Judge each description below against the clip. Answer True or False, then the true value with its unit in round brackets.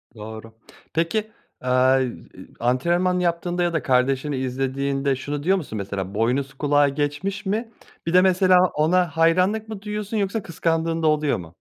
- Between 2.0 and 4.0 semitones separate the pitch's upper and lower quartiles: False (5.6 semitones)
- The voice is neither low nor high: True (155 Hz)